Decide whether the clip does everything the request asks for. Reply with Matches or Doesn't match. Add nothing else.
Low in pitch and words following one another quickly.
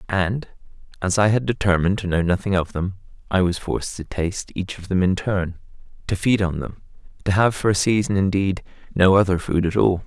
Matches